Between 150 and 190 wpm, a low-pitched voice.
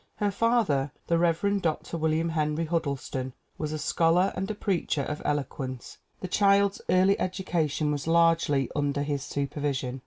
No: average, 155 wpm; medium, 160 Hz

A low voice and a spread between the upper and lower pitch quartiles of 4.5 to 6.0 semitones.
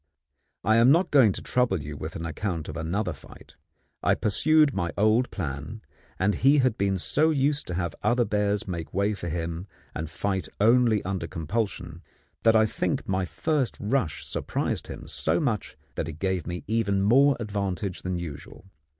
Yes: low, 100 Hz; average, 5.0 semitones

